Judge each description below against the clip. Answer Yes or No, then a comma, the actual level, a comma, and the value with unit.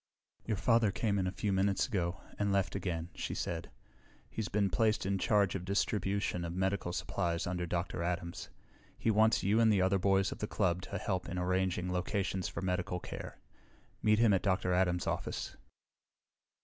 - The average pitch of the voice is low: Yes, very low, 95 Hz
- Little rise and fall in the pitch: Yes, narrow, 2.2 semitones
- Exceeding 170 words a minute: Yes, average, 180 wpm